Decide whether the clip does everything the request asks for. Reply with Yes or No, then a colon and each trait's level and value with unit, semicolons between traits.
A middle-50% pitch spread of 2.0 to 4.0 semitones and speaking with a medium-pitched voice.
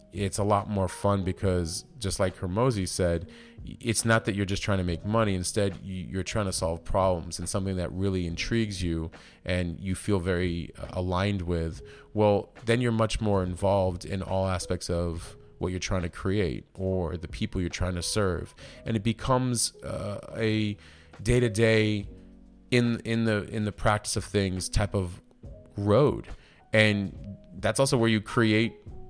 No: average, 3.3 semitones; low, 100 Hz